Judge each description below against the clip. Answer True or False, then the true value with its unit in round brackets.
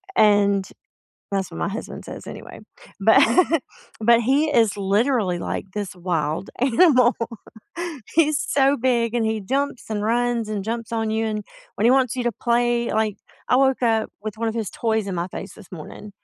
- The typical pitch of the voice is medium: False (225 Hz)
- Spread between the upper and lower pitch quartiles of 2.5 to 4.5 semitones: True (3.1 semitones)